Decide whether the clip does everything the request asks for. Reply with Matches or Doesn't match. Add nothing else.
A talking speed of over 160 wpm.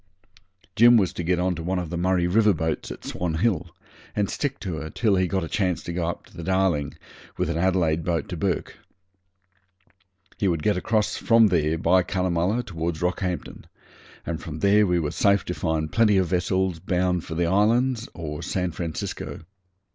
Matches